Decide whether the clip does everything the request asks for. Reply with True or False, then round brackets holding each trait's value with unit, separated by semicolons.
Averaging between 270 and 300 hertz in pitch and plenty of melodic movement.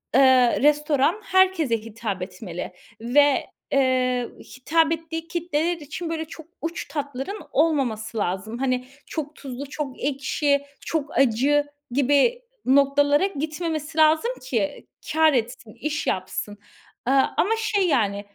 False (280 Hz; 4.3 semitones)